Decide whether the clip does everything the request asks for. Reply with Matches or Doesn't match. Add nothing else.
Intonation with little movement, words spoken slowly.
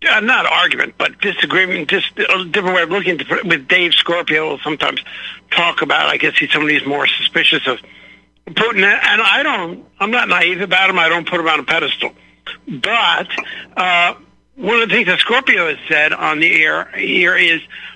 Doesn't match